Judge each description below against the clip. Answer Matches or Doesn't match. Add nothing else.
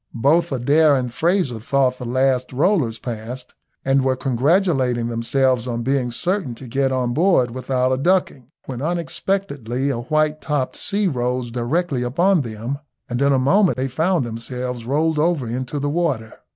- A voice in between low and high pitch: Doesn't match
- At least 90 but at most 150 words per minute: Doesn't match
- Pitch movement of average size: Matches